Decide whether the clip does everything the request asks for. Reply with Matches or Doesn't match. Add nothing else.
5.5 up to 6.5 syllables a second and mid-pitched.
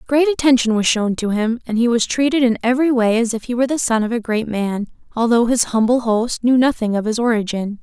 Doesn't match